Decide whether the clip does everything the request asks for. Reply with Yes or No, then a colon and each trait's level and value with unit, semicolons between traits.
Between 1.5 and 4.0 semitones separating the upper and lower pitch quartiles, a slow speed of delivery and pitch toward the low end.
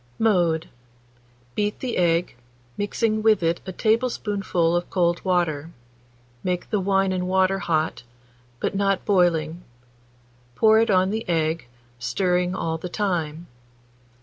No: average, 3.2 semitones; slow, 125 wpm; medium, 180 Hz